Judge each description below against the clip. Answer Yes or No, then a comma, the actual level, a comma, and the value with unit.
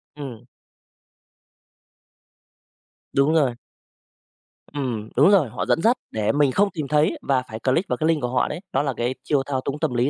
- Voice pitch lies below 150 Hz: Yes, medium, 140 Hz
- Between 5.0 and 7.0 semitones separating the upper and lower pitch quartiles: No, average, 3.3 semitones